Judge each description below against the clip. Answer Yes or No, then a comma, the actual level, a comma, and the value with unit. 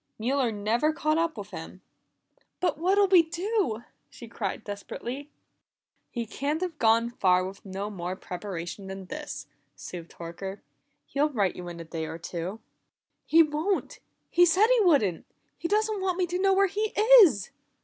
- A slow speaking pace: No, average, 165 wpm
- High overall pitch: Yes, high, 235 Hz